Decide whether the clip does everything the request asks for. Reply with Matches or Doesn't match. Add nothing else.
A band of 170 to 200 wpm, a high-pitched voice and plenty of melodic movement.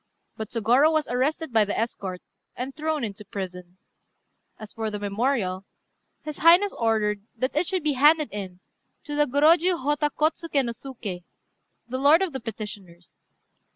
Doesn't match